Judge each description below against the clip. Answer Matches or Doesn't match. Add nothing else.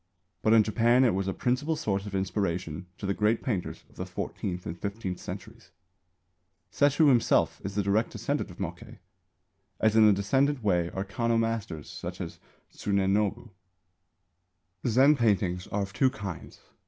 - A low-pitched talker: Matches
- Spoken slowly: Doesn't match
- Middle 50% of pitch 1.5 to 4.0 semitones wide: Matches